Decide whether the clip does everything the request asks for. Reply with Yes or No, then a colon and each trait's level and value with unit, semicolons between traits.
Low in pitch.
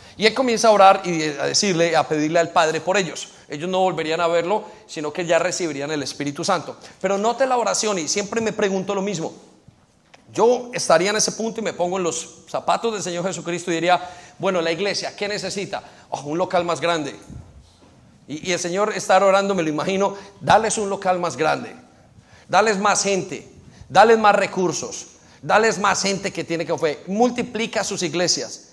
No: medium, 185 Hz